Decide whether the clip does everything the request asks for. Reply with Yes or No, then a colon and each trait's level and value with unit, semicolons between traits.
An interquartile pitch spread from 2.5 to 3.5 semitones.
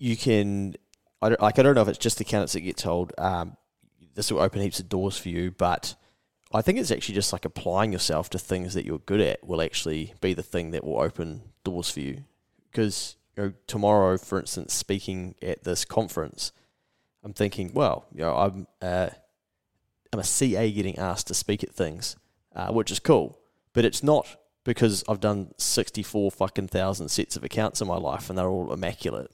Yes: average, 2.9 semitones